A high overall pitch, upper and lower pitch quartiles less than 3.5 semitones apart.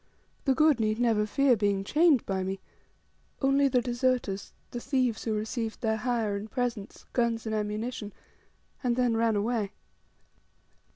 Yes: high, 230 Hz; average, 3.0 semitones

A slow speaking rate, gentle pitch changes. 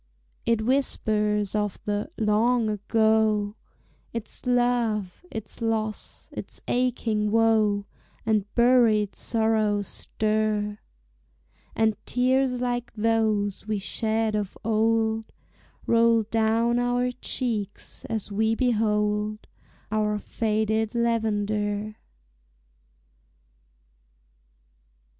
Yes: slow, 85 wpm; narrow, 1.6 semitones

